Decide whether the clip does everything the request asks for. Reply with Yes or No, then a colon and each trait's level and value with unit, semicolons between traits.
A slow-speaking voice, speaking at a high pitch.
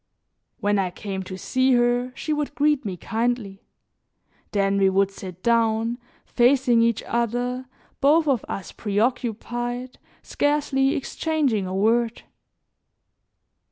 Yes: slow, 120 wpm; high, 235 Hz